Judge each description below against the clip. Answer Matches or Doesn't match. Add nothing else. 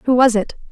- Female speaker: Matches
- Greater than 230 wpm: Matches